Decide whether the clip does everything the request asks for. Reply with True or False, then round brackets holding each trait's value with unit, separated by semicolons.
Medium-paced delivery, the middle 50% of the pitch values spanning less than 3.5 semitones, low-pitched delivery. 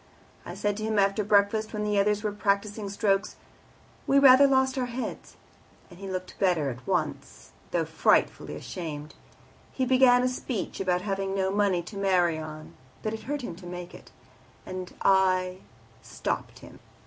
False (170 wpm; 3.1 semitones; 200 Hz)